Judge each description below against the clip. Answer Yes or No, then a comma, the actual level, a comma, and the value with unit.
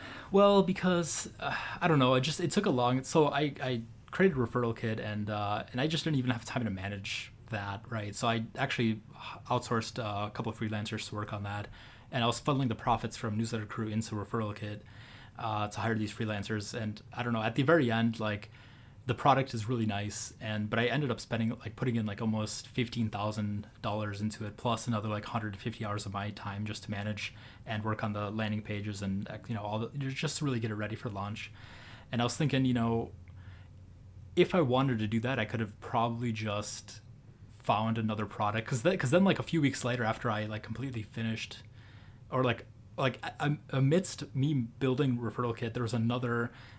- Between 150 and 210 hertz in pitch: No, low, 115 Hz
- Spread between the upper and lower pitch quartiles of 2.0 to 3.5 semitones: Yes, average, 2.9 semitones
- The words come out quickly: Yes, fast, 210 wpm